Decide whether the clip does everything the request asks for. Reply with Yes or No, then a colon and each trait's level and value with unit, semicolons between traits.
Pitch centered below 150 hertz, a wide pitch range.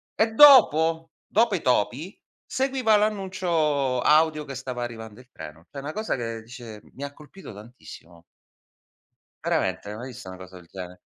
Yes: low, 135 Hz; wide, 8.5 semitones